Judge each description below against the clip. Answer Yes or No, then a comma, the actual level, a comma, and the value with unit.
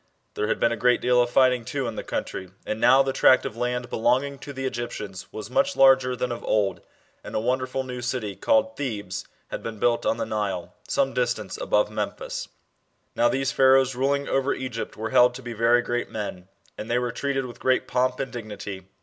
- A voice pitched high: No, low, 125 Hz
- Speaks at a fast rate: Yes, fast, 210 wpm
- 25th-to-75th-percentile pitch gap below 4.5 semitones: Yes, average, 3.0 semitones